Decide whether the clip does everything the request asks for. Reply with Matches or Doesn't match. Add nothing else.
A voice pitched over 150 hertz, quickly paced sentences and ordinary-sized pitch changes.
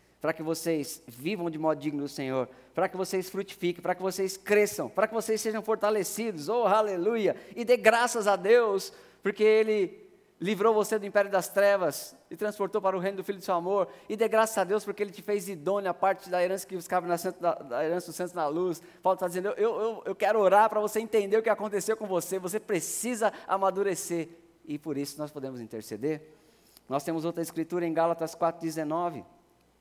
Matches